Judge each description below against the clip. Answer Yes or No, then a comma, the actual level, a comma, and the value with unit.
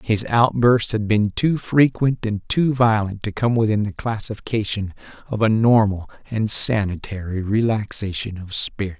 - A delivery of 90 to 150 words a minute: Yes, average, 145 wpm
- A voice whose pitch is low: Yes, low, 110 Hz